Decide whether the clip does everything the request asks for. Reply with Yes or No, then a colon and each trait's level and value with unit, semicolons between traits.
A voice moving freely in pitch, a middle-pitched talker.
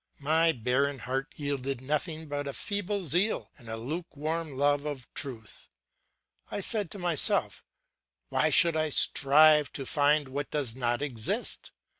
No: average, 3.1 semitones; medium, 145 Hz